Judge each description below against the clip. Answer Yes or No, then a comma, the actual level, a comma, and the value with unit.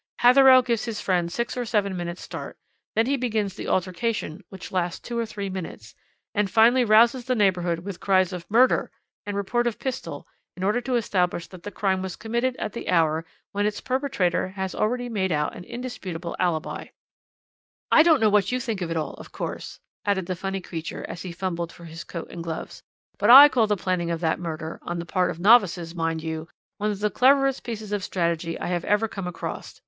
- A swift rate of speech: Yes, fast, 215 wpm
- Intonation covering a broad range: No, average, 5.0 semitones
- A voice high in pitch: Yes, high, 195 Hz